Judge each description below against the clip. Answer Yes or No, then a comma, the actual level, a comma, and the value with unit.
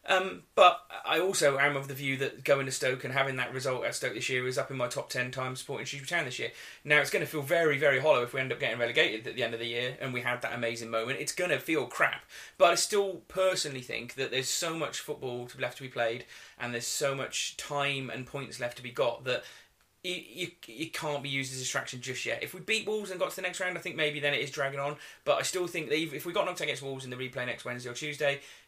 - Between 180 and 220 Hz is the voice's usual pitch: No, medium, 140 Hz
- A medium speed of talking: No, fast, 285 wpm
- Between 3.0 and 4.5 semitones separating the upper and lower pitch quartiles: Yes, average, 3.8 semitones